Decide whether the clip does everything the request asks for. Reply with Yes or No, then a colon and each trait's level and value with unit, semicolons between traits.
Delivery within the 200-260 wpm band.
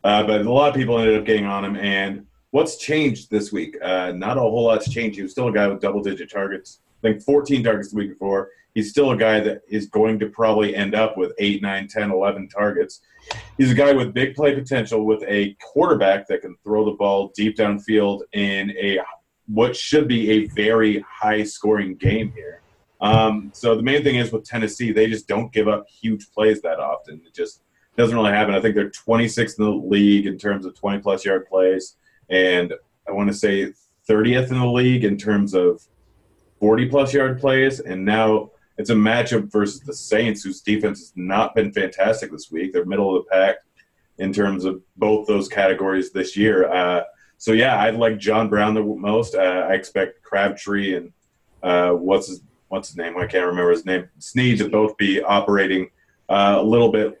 Yes: fast, 205 wpm